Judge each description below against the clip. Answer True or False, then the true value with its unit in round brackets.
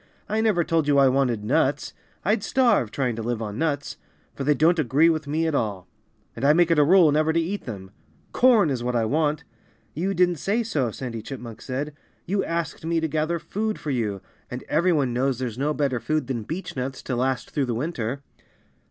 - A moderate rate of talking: False (215 wpm)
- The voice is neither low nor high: True (145 Hz)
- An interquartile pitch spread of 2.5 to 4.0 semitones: False (5.0 semitones)